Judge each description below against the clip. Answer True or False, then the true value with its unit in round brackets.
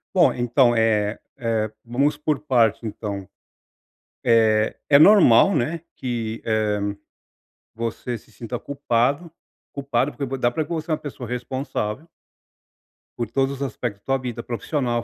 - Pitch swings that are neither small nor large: True (3.7 semitones)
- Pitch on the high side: False (120 Hz)